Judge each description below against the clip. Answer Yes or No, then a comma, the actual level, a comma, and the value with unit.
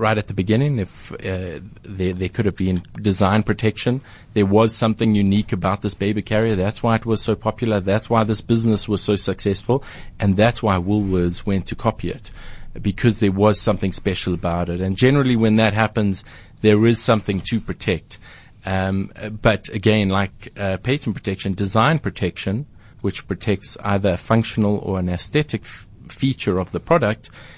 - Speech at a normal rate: Yes, average, 175 wpm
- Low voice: Yes, low, 105 Hz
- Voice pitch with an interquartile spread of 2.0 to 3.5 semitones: Yes, average, 2.7 semitones